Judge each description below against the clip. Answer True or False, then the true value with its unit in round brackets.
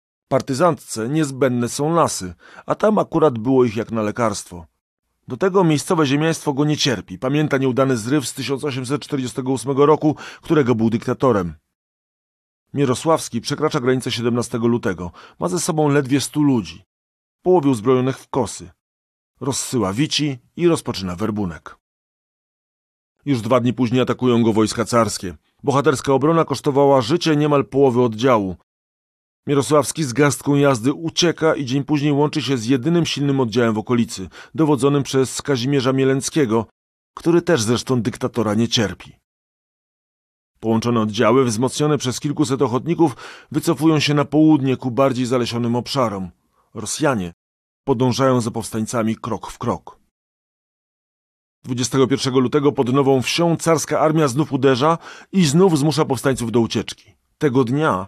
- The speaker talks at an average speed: True (130 wpm)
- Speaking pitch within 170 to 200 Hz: False (135 Hz)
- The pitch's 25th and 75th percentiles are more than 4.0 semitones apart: True (4.4 semitones)